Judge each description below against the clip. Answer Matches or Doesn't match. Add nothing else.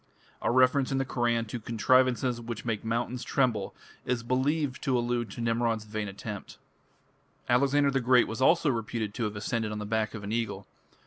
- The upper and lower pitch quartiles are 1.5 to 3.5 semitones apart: Matches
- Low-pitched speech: Matches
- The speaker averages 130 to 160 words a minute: Doesn't match